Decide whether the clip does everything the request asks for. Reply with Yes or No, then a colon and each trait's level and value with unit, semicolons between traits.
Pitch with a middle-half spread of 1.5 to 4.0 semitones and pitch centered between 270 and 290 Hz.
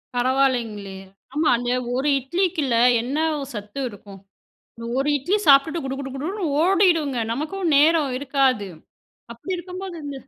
No: average, 5.0 semitones; very high, 275 Hz